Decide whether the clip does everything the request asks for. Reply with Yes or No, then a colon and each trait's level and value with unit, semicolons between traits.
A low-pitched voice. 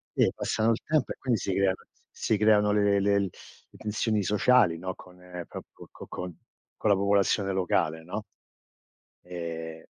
Yes: low, 100 Hz